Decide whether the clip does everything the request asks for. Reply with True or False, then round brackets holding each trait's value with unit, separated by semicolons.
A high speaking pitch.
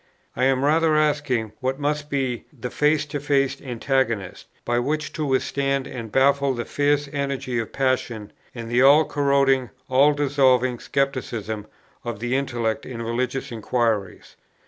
False (135 Hz)